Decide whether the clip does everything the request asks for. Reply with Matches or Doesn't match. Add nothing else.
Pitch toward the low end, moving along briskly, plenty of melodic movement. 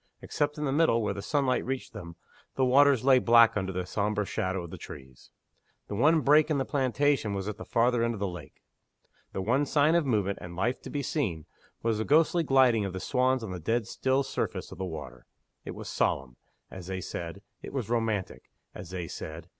Matches